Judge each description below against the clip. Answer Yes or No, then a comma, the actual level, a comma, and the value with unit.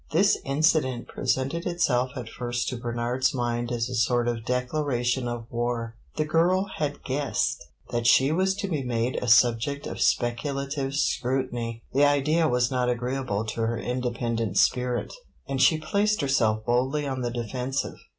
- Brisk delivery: No, average, 160 wpm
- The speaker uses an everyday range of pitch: Yes, average, 3.0 semitones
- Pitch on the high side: No, low, 125 Hz